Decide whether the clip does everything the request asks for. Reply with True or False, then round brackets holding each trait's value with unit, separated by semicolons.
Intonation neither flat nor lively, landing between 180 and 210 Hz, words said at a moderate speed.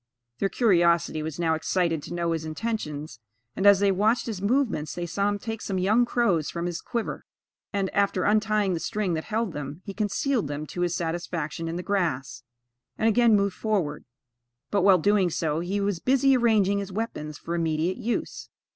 True (4.3 semitones; 185 Hz; 190 wpm)